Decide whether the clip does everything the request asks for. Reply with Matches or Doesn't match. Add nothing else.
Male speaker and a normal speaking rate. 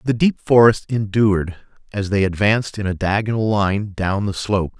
Matches